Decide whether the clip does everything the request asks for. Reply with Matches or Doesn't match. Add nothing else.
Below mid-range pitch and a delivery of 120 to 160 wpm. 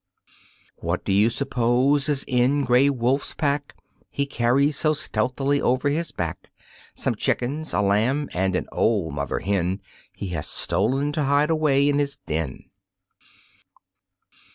Matches